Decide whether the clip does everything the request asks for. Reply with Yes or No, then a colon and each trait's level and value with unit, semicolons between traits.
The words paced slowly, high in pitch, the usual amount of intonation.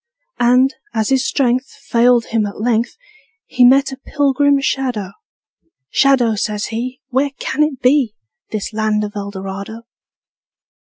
Yes: slow, 130 wpm; high, 245 Hz; average, 3.8 semitones